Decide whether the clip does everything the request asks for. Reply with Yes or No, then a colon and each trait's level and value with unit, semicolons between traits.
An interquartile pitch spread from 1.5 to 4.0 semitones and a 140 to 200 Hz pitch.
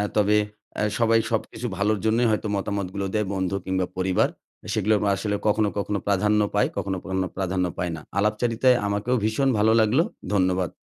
No: narrow, 2.4 semitones; low, 105 Hz